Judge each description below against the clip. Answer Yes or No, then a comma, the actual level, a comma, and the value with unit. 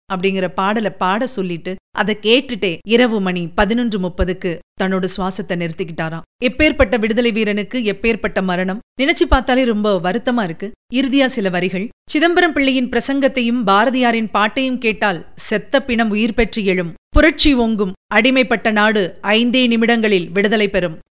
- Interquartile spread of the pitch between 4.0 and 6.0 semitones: Yes, average, 4.4 semitones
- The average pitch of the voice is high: Yes, high, 215 Hz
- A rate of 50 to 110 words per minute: No, average, 125 wpm